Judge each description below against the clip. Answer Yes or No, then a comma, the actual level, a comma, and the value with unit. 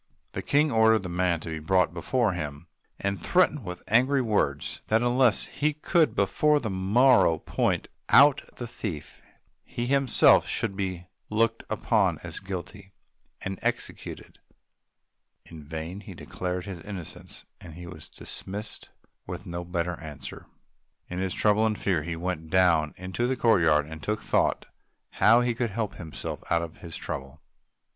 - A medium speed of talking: Yes, average, 150 wpm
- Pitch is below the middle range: Yes, very low, 95 Hz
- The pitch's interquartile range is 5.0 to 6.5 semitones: Yes, average, 5.3 semitones